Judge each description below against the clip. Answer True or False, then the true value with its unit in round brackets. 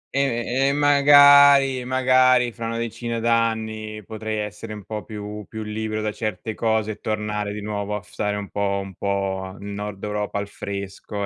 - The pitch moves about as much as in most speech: False (2.3 semitones)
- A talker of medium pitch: False (110 Hz)